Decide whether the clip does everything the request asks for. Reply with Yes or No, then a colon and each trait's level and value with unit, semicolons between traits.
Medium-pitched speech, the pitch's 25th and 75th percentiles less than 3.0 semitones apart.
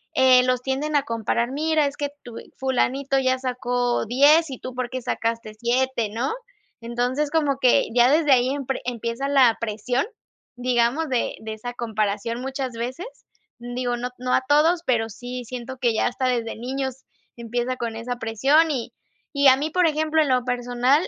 No: very high, 250 Hz; narrow, 2.4 semitones